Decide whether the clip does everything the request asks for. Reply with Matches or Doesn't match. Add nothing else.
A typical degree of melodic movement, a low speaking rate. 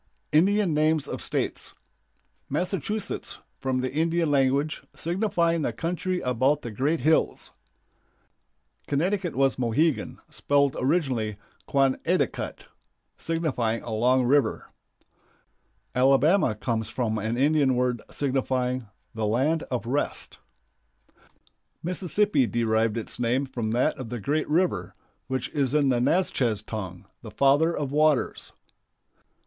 Matches